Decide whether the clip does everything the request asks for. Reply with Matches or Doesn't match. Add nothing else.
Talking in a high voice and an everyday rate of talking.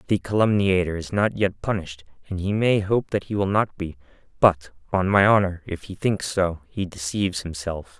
Doesn't match